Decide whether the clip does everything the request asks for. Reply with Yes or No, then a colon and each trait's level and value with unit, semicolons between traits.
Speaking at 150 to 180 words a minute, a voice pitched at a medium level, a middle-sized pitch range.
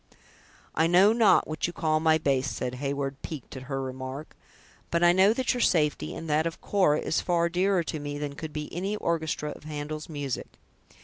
No: average, 200 wpm; medium, 155 Hz; average, 3.3 semitones